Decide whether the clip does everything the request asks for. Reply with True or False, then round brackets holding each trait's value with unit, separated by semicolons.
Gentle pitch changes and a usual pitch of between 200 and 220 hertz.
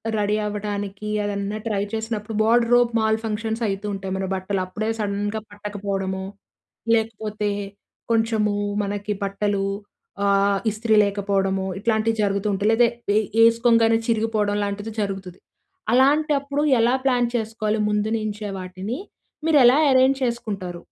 True (2.2 semitones; 210 Hz)